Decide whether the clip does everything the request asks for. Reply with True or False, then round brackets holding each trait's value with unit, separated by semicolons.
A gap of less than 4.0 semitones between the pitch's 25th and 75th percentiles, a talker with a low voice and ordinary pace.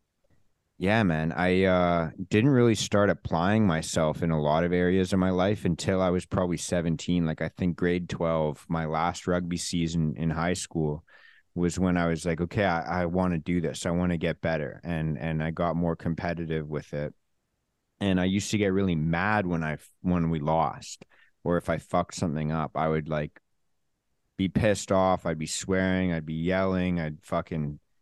True (2.4 semitones; 85 Hz; 195 wpm)